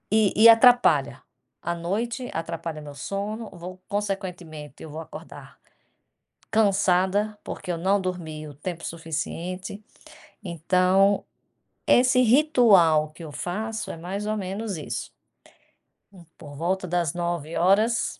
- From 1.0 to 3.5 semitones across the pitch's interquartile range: No, average, 4.0 semitones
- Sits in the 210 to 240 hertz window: No, medium, 185 Hz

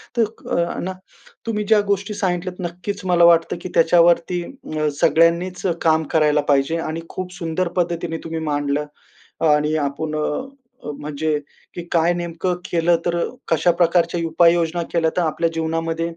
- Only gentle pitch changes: Yes, narrow, 1.7 semitones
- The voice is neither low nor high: Yes, medium, 170 Hz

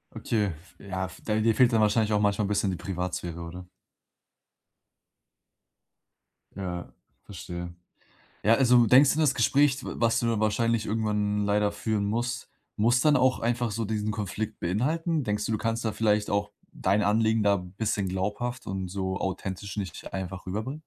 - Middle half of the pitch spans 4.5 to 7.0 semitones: No, average, 2.9 semitones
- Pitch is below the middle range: Yes, low, 105 Hz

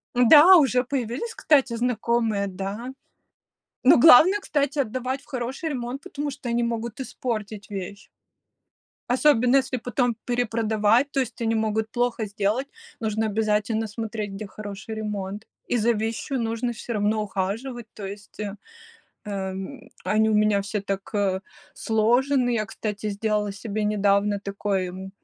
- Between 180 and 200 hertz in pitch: No, high, 220 Hz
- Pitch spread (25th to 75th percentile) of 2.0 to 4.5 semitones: Yes, average, 3.1 semitones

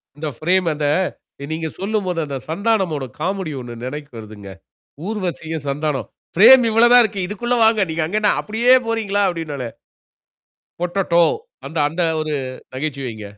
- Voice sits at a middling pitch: Yes, medium, 170 Hz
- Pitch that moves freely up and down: Yes, wide, 5.9 semitones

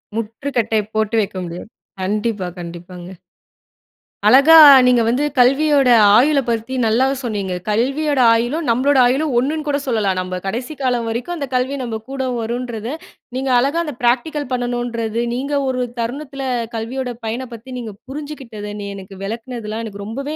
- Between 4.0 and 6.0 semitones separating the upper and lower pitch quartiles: No, average, 3.6 semitones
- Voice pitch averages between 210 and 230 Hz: No, high, 240 Hz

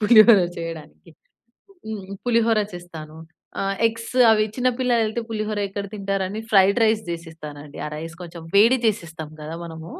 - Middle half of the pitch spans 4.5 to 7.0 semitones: Yes, average, 5.0 semitones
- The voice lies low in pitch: No, high, 195 Hz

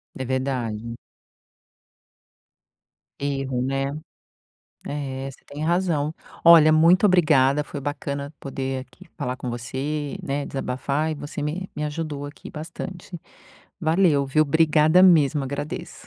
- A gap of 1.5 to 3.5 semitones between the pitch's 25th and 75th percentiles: Yes, narrow, 2.6 semitones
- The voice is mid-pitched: Yes, medium, 145 Hz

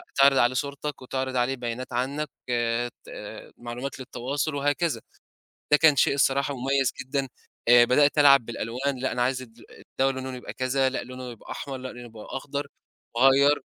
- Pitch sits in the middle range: No, low, 130 Hz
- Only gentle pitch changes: Yes, narrow, 2.1 semitones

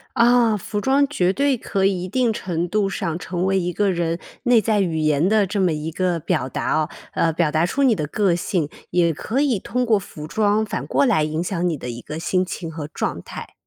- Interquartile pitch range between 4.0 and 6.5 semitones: Yes, average, 4.7 semitones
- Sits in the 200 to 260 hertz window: No, medium, 185 Hz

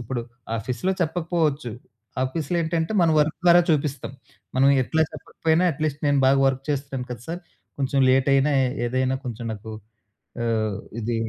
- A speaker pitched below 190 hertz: Yes, medium, 140 Hz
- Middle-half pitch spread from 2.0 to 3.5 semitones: No, average, 4.1 semitones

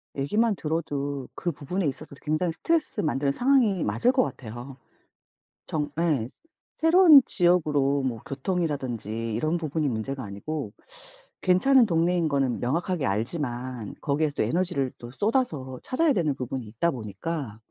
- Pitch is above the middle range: No, medium, 150 Hz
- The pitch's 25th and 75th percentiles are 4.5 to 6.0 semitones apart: Yes, wide, 5.6 semitones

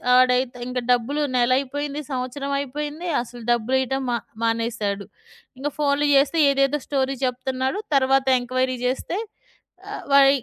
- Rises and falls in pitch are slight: Yes, narrow, 2.0 semitones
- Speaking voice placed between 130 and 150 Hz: No, very high, 265 Hz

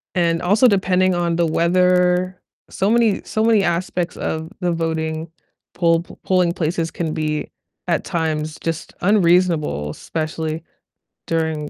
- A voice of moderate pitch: Yes, medium, 170 Hz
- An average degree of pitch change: No, narrow, 2.3 semitones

